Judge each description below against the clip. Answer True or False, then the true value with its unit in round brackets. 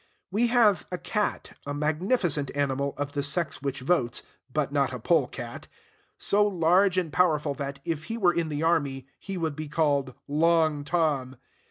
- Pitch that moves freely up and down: False (3.7 semitones)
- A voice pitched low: False (155 Hz)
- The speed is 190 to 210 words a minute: False (175 wpm)